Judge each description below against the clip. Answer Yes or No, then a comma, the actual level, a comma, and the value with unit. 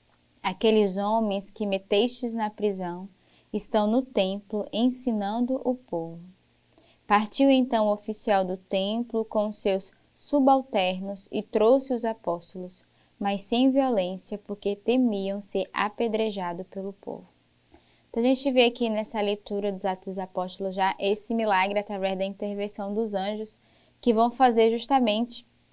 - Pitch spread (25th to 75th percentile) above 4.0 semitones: No, average, 3.0 semitones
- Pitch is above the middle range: Yes, high, 210 Hz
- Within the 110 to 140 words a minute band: Yes, average, 135 wpm